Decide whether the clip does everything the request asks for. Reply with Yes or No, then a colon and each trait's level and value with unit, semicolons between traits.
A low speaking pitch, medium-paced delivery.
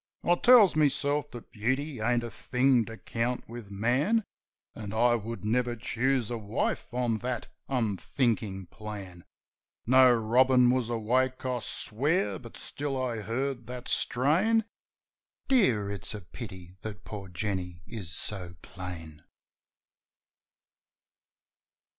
No: low, 120 Hz; slow, 125 wpm